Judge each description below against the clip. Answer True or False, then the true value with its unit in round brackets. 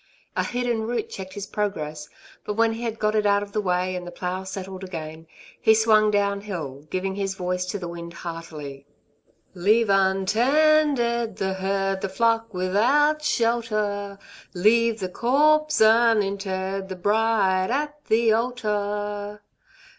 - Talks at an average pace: True (145 wpm)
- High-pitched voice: True (205 Hz)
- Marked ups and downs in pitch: False (3.4 semitones)